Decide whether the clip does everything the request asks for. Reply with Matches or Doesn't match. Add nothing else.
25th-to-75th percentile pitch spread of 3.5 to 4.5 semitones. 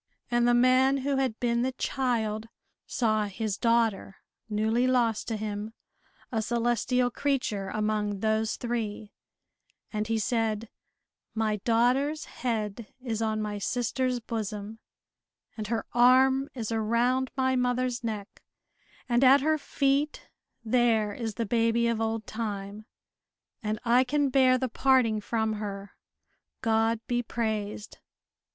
Doesn't match